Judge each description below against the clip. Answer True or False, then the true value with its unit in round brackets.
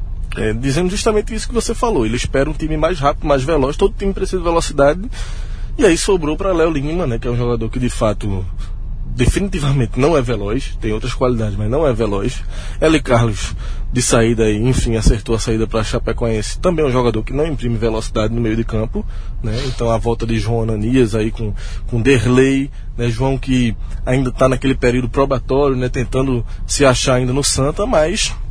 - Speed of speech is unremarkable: False (200 wpm)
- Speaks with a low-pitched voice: True (125 Hz)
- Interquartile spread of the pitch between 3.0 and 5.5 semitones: True (3.8 semitones)